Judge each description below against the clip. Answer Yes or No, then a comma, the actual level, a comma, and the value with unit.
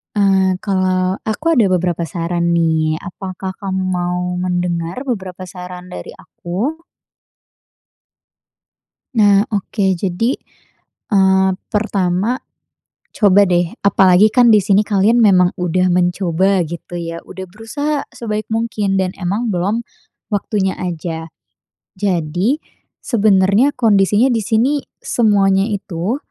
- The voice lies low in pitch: No, high, 190 Hz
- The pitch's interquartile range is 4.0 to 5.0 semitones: No, average, 3.1 semitones